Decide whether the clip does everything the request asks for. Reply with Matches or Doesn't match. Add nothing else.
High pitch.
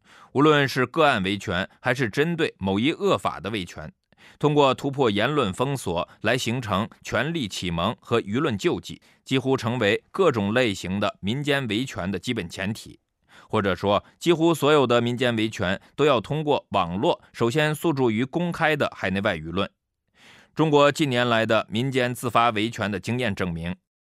Doesn't match